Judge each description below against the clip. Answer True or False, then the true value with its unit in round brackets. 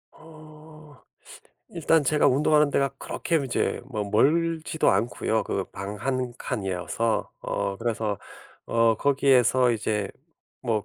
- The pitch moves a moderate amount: False (5.8 semitones)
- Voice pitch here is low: True (125 Hz)